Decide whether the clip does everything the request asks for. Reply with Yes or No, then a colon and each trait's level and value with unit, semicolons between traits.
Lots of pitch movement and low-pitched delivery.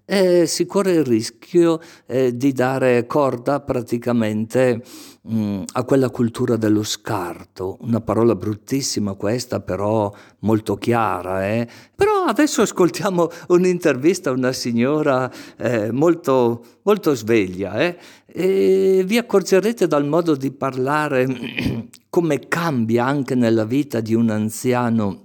Yes: wide, 6.6 semitones; low, 130 Hz